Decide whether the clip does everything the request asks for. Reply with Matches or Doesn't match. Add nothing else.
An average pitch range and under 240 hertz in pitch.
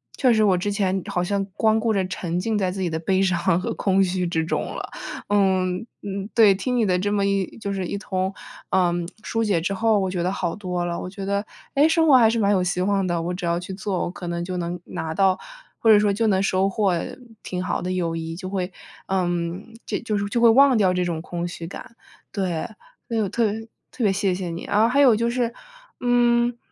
Matches